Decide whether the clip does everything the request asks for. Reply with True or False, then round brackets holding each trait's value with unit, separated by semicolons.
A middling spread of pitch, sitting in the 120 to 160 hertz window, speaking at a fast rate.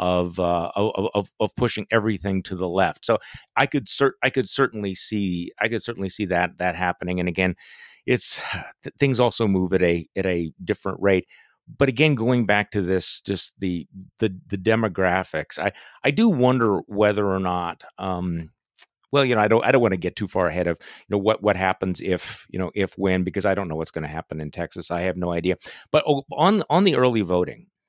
False (4.1 semitones; 95 Hz; 215 wpm)